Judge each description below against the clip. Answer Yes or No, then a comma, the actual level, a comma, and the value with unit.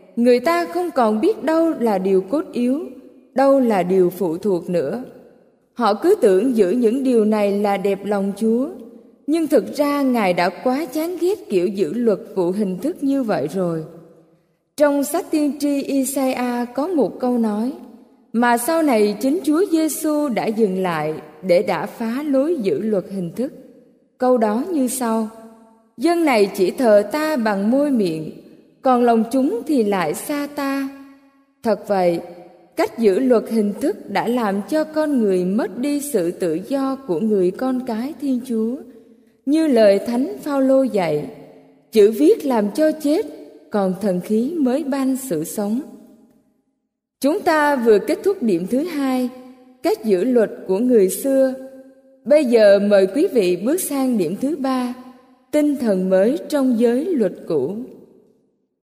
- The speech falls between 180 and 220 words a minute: No, slow, 165 wpm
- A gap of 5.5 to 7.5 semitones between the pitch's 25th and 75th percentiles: No, average, 5.1 semitones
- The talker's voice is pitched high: Yes, high, 245 Hz